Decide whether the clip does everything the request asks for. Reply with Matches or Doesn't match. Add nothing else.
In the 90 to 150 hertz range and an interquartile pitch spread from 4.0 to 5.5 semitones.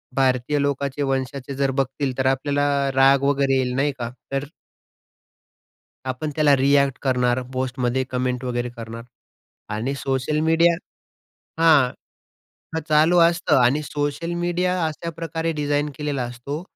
Doesn't match